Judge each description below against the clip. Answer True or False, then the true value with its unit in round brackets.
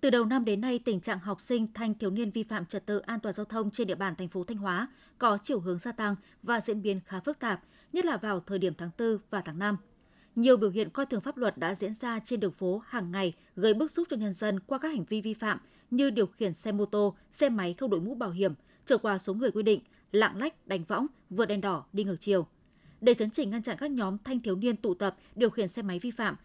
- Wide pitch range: False (3.3 semitones)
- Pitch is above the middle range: True (215 Hz)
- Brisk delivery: True (275 wpm)